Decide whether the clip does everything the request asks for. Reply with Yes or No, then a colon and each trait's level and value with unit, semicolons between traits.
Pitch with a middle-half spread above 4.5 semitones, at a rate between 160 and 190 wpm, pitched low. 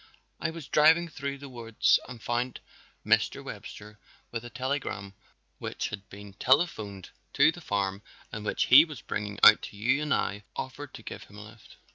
Yes: wide, 5.4 semitones; average, 180 wpm; low, 115 Hz